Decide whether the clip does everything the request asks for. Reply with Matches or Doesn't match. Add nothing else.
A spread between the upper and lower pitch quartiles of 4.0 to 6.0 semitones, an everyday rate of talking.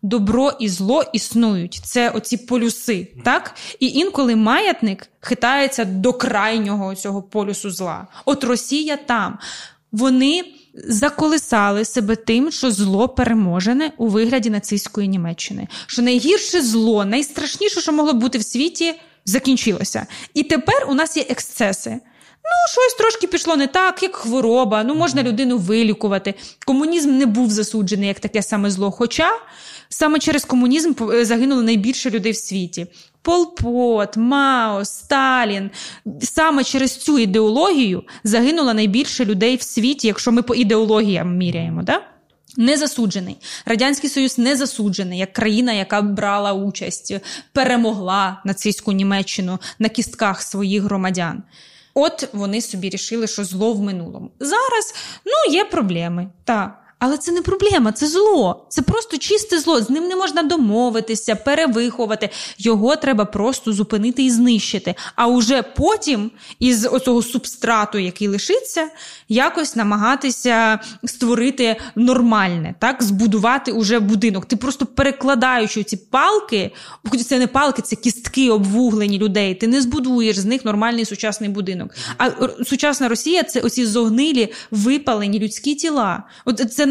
Matches